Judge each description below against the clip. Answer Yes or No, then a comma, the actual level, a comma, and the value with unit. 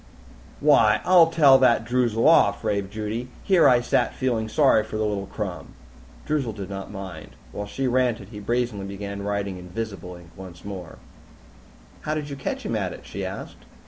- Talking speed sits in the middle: Yes, average, 180 wpm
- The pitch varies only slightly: No, average, 4.2 semitones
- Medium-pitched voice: No, low, 105 Hz